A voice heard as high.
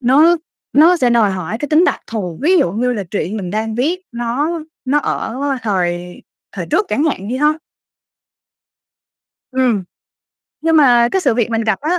Yes: high, 240 Hz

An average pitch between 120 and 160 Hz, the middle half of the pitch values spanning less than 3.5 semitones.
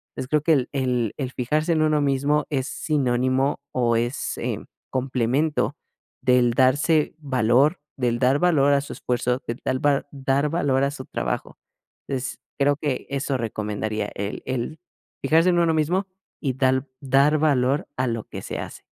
Yes: low, 135 Hz; average, 2.9 semitones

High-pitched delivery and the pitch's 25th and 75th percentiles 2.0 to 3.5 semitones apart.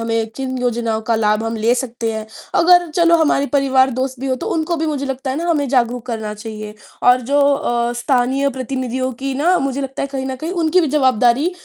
Yes: very high, 260 Hz; average, 2.9 semitones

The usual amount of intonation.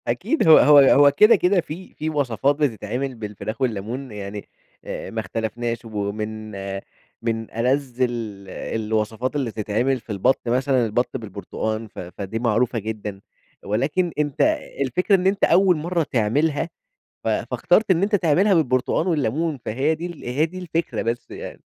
No: wide, 6.1 semitones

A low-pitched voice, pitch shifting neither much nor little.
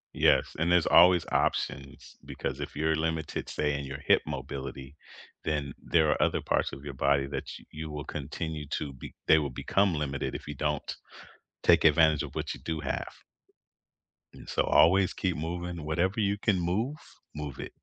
Yes: very low, 75 Hz; average, 3.4 semitones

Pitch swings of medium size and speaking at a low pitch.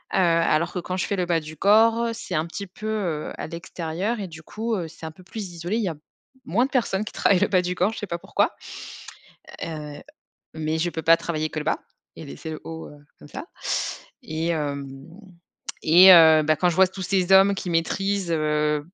No: average, 3.5 semitones; medium, 170 Hz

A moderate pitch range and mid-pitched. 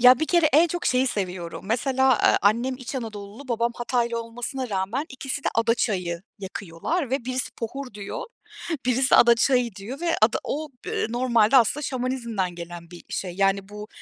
No: average, 4.5 semitones; high, 235 Hz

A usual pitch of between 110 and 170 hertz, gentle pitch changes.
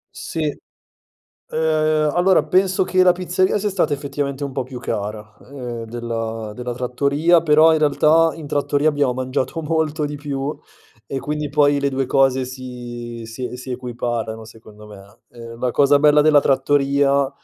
No: medium, 140 Hz; average, 3.8 semitones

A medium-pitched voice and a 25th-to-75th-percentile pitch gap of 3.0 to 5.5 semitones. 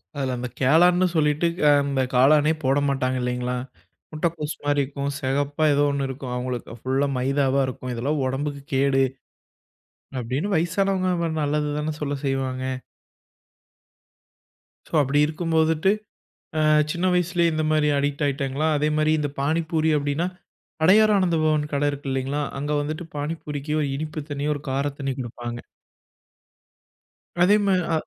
No: medium, 145 Hz; narrow, 2.6 semitones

